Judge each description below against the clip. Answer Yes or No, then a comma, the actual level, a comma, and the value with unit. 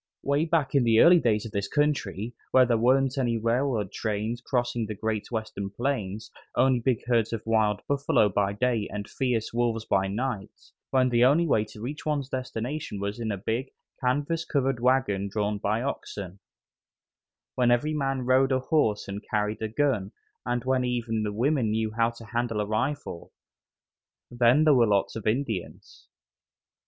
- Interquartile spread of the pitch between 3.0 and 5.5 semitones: Yes, average, 3.6 semitones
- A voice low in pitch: Yes, low, 120 Hz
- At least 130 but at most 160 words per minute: No, average, 175 wpm